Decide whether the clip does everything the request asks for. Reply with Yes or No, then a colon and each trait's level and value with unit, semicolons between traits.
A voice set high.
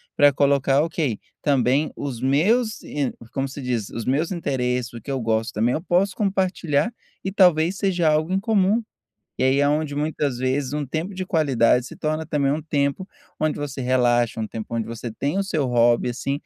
No: medium, 145 Hz